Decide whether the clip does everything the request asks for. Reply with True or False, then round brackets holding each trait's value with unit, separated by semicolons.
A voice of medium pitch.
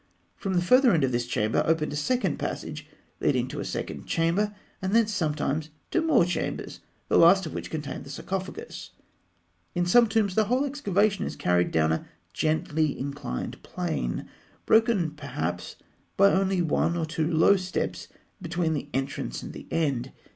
True (170 Hz)